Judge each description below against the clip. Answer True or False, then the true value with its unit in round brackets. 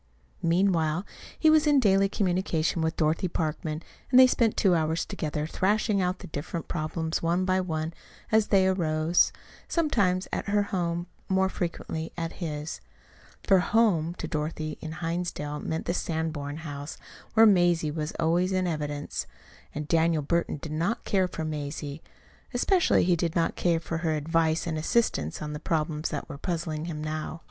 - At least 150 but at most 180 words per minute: True (165 wpm)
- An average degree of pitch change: True (3.1 semitones)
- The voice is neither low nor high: True (165 Hz)